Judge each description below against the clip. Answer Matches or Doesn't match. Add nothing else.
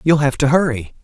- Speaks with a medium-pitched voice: Matches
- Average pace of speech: Doesn't match